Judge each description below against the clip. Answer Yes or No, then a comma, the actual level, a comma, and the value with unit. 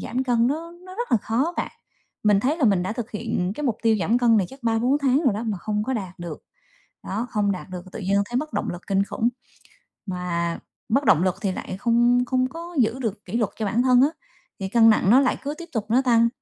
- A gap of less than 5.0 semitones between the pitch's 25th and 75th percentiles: Yes, average, 4.3 semitones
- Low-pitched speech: No, high, 230 Hz